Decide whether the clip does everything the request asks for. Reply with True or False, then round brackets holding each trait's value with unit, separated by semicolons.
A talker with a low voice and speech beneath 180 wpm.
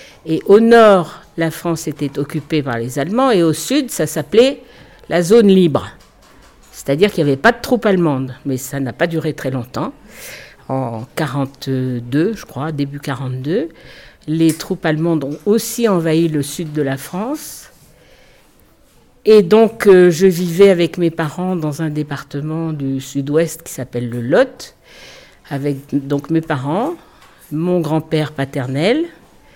False (155 Hz; 150 wpm)